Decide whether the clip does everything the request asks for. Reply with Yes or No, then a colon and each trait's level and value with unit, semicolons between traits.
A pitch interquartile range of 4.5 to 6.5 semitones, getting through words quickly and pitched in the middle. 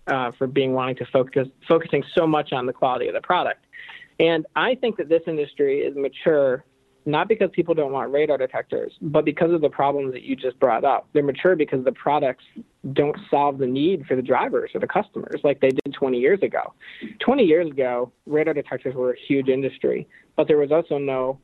Yes: average, 5.3 semitones; fast, 210 wpm; medium, 150 Hz